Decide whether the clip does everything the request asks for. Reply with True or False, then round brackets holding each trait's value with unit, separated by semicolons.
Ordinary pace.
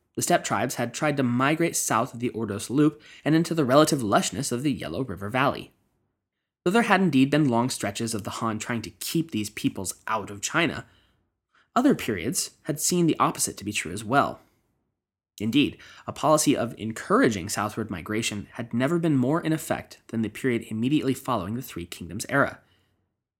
True (185 wpm)